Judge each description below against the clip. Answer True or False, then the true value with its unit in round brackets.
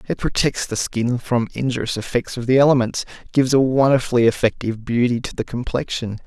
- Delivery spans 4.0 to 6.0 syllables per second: True (5.9 syllables/s)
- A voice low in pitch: True (120 Hz)